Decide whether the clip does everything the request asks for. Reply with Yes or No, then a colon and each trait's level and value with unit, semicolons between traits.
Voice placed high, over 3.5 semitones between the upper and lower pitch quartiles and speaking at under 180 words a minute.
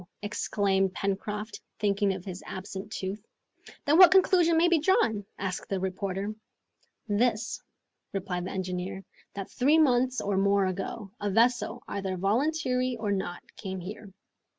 Yes: high, 200 Hz; average, 4.2 semitones; average, 140 wpm